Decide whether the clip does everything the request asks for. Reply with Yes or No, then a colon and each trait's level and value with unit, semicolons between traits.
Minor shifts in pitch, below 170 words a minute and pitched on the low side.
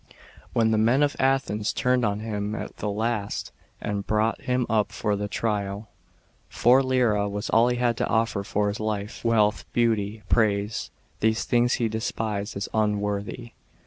Yes: narrow, 2.3 semitones; average, 155 wpm; low, 110 Hz